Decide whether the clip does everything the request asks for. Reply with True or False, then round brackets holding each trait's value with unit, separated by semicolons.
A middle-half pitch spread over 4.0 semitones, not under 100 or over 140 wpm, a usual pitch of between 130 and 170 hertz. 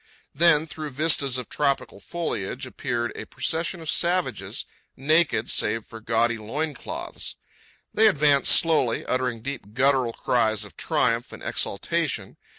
True (5.4 semitones; 135 wpm; 135 Hz)